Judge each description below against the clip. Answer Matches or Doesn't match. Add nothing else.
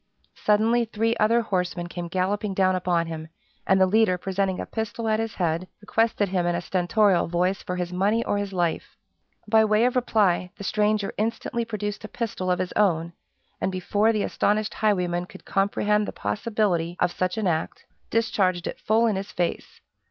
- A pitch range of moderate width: Matches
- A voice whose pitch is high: Matches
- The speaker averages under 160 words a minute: Doesn't match